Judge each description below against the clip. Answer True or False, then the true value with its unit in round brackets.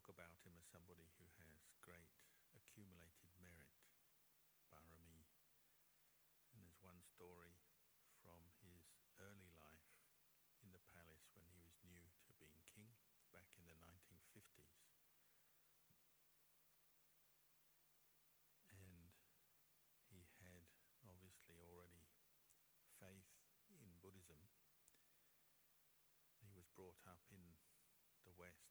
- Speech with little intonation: True (2.0 semitones)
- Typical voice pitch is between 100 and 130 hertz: False (85 Hz)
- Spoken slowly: True (100 wpm)